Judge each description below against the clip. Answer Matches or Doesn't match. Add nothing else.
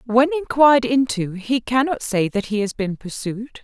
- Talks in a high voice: Matches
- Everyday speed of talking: Matches